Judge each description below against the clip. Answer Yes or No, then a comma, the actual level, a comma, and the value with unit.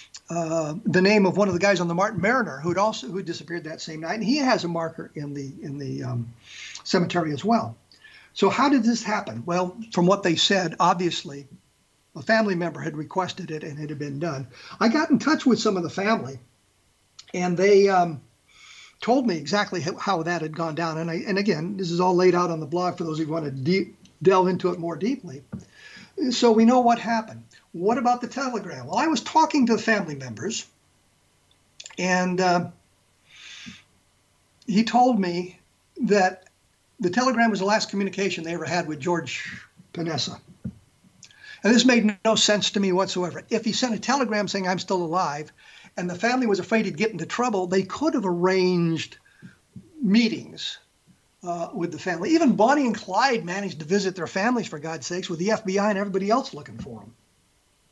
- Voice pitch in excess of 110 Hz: Yes, medium, 185 Hz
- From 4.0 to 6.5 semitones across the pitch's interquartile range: Yes, average, 4.6 semitones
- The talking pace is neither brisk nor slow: Yes, average, 195 wpm